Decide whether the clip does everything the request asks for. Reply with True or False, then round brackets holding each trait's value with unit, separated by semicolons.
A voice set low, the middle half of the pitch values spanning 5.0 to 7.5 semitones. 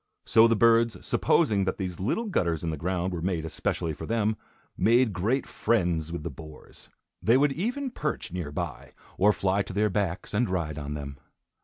True (95 Hz; 5.5 semitones)